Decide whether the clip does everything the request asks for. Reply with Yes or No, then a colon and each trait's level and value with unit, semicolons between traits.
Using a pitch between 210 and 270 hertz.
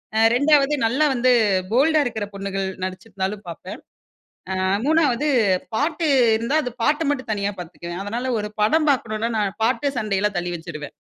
Yes: high, 225 Hz